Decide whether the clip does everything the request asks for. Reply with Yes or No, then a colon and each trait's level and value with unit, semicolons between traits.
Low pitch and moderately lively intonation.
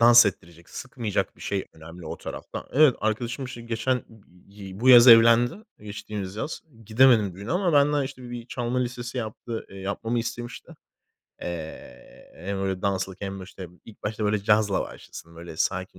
Yes: low, 110 Hz; average, 3.9 semitones